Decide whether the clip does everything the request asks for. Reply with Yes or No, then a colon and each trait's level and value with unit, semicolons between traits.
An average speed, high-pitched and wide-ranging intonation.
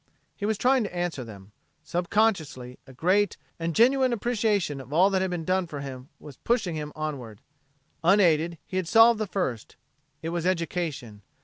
No: average, 180 wpm; medium, 175 Hz; wide, 5.7 semitones